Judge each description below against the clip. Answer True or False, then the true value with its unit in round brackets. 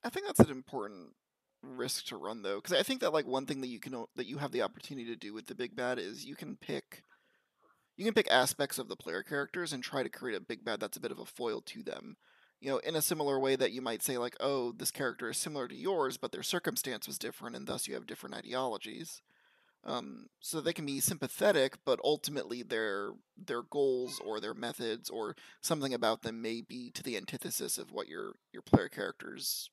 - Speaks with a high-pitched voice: False (135 Hz)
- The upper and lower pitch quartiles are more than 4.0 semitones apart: True (4.7 semitones)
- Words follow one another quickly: True (235 wpm)